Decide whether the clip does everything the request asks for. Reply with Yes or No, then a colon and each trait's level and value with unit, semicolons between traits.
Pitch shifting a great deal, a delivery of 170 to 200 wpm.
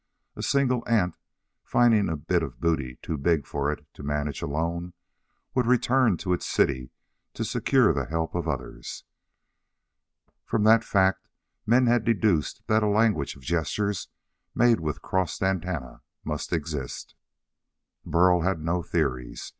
No: wide, 6.5 semitones; average, 145 wpm